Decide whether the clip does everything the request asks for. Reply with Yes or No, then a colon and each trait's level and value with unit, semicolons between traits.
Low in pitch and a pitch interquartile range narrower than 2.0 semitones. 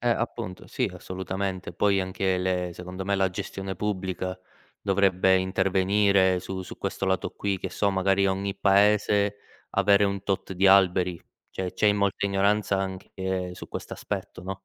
Yes: very low, 95 Hz; narrow, 1.2 semitones